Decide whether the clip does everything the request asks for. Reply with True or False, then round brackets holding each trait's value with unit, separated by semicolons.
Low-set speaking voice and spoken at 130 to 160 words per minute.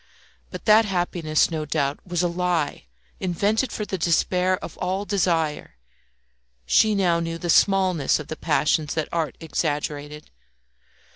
False (170 Hz; 140 wpm)